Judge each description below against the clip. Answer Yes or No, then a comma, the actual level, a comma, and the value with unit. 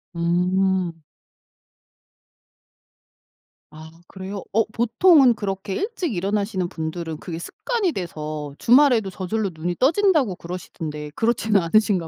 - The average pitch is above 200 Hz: No, high, 190 Hz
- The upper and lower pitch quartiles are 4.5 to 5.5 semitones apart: Yes, average, 5.1 semitones